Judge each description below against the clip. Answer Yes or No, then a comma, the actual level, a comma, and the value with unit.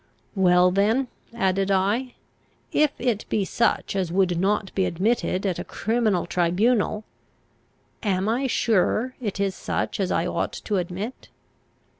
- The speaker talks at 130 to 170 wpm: Yes, average, 140 wpm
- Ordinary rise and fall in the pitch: Yes, average, 3.6 semitones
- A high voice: Yes, high, 200 Hz